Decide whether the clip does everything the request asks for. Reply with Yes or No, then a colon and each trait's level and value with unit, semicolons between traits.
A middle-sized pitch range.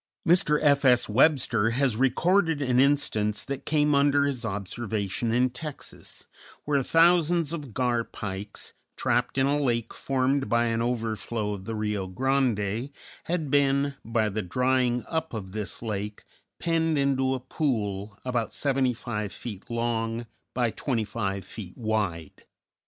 Yes: average, 4.5 semitones